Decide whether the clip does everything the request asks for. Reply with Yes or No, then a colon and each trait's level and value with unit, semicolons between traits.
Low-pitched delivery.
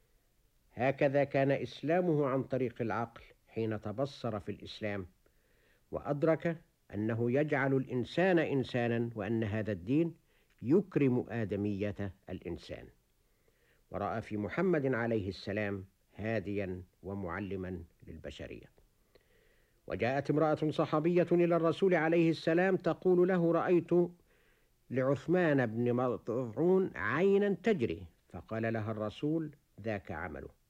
Yes: low, 125 Hz